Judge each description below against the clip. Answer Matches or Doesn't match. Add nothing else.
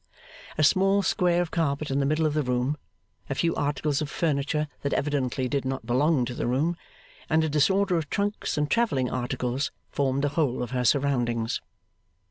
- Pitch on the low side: Doesn't match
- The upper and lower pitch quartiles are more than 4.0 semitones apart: Doesn't match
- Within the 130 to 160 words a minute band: Doesn't match